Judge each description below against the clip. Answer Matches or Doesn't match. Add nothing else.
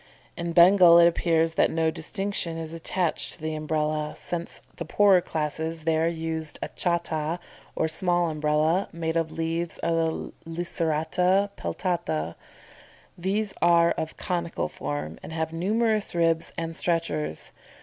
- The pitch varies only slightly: Matches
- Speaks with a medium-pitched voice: Matches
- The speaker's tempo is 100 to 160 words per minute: Matches